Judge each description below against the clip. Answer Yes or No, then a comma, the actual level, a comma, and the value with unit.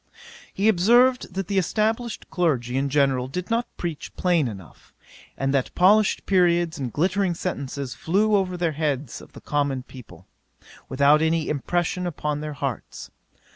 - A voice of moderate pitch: Yes, medium, 160 Hz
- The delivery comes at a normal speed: Yes, average, 150 wpm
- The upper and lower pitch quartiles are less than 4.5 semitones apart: No, average, 5.2 semitones